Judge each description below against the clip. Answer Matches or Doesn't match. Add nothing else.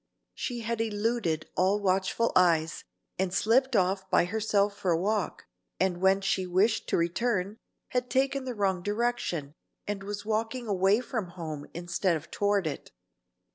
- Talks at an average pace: Matches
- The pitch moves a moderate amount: Matches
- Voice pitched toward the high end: Matches